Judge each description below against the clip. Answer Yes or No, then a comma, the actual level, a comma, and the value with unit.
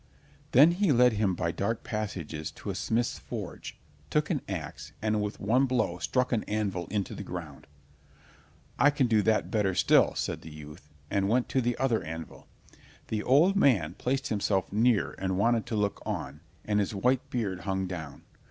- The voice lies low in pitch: Yes, low, 105 Hz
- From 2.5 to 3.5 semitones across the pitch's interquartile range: No, average, 4.7 semitones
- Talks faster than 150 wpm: Yes, average, 180 wpm